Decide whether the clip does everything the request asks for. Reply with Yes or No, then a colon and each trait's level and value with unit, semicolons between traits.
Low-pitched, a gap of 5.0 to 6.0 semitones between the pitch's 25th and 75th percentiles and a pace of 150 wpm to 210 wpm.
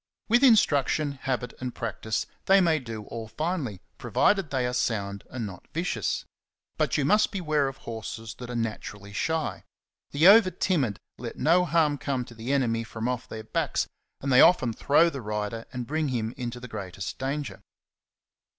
Yes: low, 125 Hz; wide, 5.5 semitones; average, 175 wpm